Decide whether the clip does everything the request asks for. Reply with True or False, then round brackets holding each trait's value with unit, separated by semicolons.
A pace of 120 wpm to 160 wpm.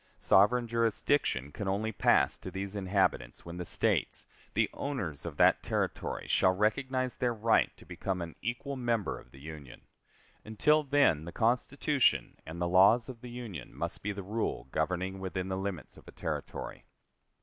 False (170 wpm)